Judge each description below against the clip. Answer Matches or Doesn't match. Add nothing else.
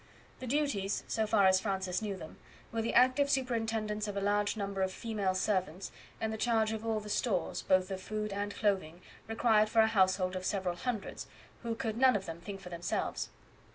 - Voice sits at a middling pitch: Doesn't match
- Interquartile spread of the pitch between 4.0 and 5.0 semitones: Doesn't match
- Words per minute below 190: Doesn't match